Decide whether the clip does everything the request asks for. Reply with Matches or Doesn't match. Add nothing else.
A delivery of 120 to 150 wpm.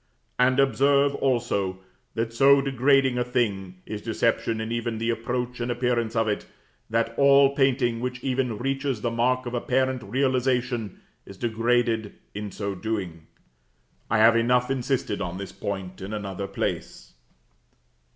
Matches